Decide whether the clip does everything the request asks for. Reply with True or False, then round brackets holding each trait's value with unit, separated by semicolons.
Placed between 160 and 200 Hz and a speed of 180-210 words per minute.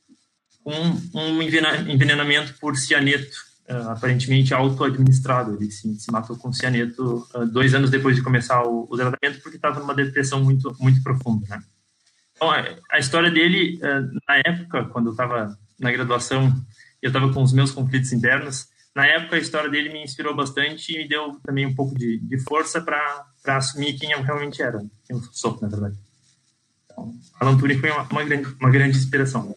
False (135 Hz; 185 wpm)